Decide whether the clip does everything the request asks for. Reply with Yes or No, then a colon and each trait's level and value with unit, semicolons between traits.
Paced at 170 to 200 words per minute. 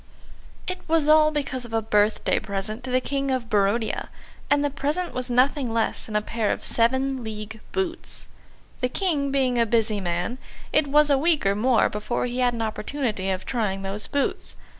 Yes: average, 190 wpm